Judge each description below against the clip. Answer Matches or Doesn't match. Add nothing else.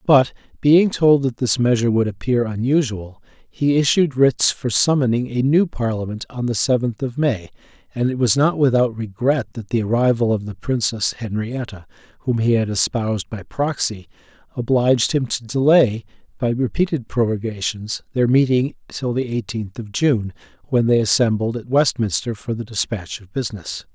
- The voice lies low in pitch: Matches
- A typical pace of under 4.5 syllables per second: Doesn't match